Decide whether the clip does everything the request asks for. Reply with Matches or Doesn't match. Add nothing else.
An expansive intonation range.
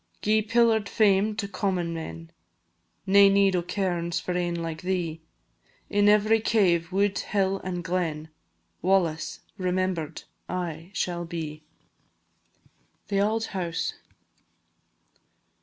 Doesn't match